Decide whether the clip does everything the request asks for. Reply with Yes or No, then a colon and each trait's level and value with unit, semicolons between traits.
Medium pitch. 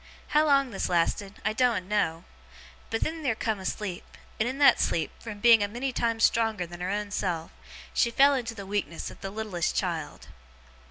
No: high, 210 Hz